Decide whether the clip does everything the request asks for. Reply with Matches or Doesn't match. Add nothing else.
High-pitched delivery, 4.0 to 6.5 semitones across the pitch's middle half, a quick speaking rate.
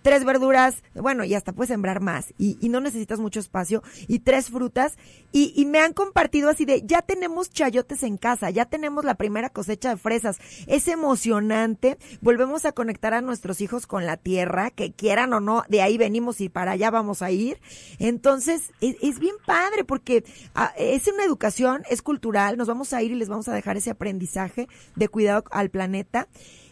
Matches